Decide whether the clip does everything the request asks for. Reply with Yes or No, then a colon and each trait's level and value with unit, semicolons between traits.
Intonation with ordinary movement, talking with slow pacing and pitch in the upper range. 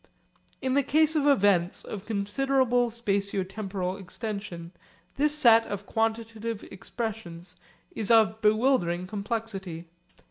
Yes: average, 3.5 semitones; slow, 110 wpm; high, 215 Hz